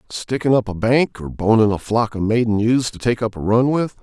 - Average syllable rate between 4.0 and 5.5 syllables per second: Yes, 5.3 syllables/s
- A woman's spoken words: No, male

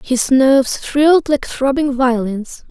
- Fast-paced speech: No, slow, 135 wpm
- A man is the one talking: No, female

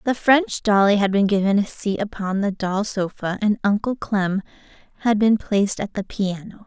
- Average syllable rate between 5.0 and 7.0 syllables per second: No, 4.8 syllables/s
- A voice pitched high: Yes, high, 205 Hz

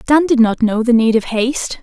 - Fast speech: Yes, fast, 265 wpm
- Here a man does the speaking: No, female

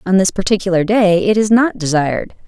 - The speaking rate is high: No, average, 195 wpm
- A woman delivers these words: Yes, female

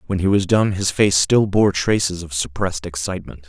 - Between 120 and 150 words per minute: No, fast, 205 wpm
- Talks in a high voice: No, very low, 90 Hz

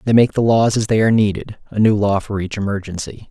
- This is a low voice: Yes, low, 105 Hz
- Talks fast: Yes, fast, 255 wpm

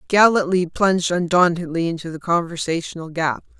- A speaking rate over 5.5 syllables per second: No, 5.4 syllables/s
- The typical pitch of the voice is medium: Yes, medium, 175 Hz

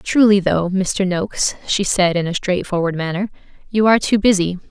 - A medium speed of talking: Yes, average, 180 wpm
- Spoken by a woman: Yes, female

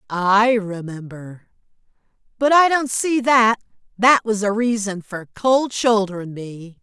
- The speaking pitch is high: Yes, high, 215 Hz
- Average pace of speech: No, slow, 130 wpm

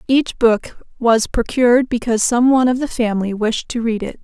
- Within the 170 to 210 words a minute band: Yes, average, 200 wpm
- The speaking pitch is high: Yes, high, 235 Hz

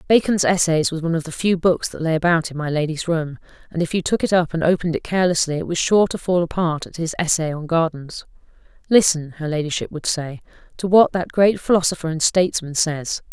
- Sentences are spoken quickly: Yes, fast, 220 wpm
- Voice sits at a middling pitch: Yes, medium, 165 Hz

